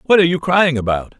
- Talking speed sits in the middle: No, fast, 250 wpm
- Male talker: Yes, male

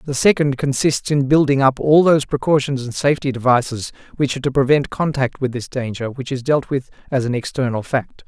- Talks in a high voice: No, low, 135 Hz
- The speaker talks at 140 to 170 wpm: No, fast, 205 wpm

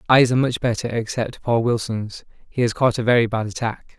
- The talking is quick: Yes, fast, 210 wpm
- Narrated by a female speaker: No, male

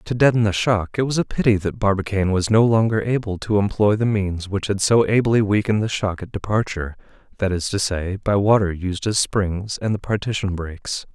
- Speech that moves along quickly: Yes, fast, 215 wpm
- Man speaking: Yes, male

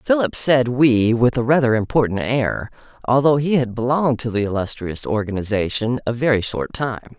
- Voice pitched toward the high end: No, low, 125 Hz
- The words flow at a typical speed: Yes, average, 165 wpm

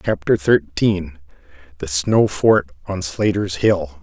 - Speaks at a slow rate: Yes, slow, 105 wpm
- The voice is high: No, low, 105 Hz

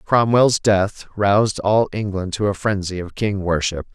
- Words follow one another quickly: No, average, 165 wpm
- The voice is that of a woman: No, male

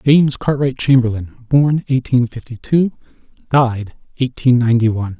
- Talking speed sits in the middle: No, slow, 125 wpm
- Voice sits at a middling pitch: No, low, 125 Hz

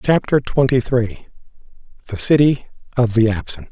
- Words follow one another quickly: No, slow, 115 wpm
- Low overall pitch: Yes, low, 130 Hz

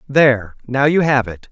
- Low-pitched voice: Yes, low, 130 Hz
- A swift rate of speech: No, average, 195 wpm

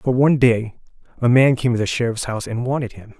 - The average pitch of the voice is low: Yes, low, 120 Hz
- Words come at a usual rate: No, fast, 245 wpm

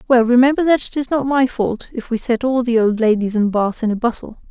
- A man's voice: No, female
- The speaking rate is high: Yes, fast, 265 wpm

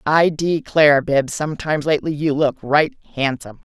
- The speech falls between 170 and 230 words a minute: No, average, 145 wpm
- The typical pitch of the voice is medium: Yes, medium, 150 Hz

